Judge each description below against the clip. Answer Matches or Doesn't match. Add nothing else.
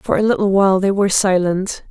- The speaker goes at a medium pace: Doesn't match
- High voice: Matches